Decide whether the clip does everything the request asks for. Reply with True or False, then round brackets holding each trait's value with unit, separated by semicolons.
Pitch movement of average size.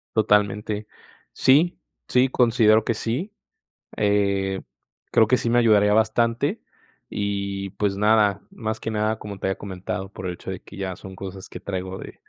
False (2.3 semitones)